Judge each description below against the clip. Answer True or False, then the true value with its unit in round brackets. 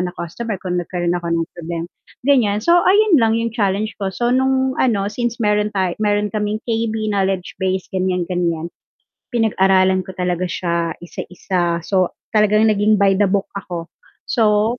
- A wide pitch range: False (3.6 semitones)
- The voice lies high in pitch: True (200 Hz)